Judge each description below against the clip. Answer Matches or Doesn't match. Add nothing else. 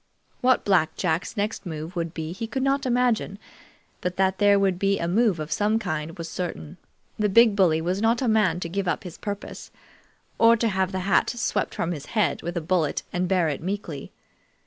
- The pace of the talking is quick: Matches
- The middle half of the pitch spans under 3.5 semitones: Doesn't match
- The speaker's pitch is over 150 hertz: Matches